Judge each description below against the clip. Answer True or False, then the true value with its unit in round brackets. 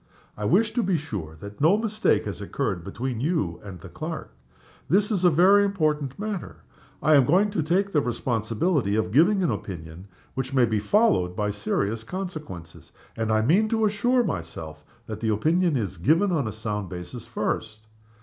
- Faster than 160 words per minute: True (180 wpm)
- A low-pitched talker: True (130 Hz)